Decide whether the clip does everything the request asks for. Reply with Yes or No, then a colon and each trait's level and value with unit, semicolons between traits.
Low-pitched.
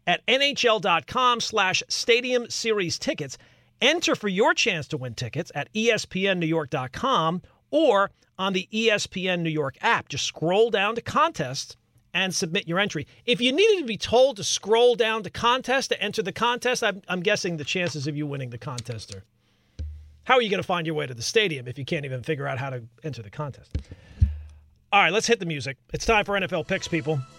No: medium, 175 Hz